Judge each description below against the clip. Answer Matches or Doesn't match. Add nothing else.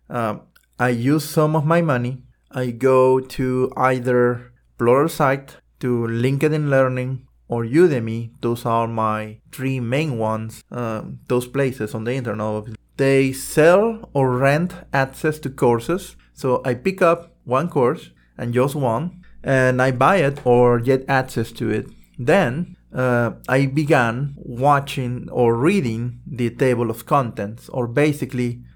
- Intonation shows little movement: Doesn't match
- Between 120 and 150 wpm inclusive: Matches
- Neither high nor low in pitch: Doesn't match